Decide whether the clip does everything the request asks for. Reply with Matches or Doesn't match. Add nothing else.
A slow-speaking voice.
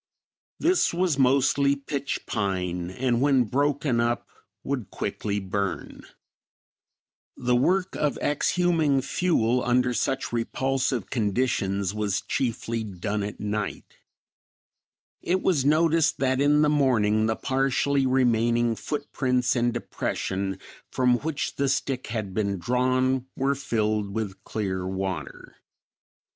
Matches